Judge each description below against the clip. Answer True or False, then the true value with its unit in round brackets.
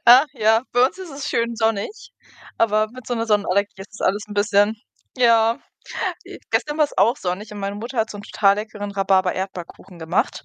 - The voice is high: True (215 Hz)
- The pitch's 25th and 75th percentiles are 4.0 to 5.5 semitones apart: False (2.8 semitones)